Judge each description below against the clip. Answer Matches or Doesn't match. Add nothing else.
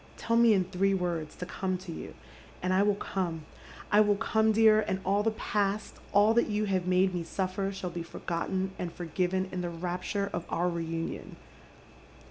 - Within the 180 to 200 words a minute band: Matches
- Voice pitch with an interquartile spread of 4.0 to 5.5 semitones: Doesn't match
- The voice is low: Doesn't match